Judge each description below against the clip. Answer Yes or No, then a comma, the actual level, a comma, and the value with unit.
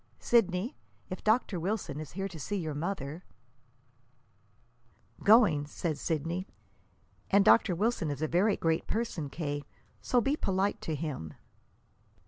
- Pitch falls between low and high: Yes, medium, 170 Hz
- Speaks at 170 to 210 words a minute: No, slow, 135 wpm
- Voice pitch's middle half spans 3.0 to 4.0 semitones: No, wide, 5.5 semitones